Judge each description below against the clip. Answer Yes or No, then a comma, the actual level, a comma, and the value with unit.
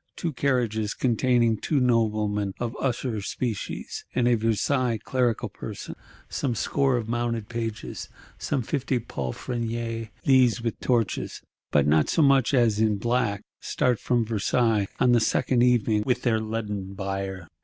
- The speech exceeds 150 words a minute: No, average, 145 wpm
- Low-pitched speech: Yes, low, 115 Hz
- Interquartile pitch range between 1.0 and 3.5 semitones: Yes, average, 2.7 semitones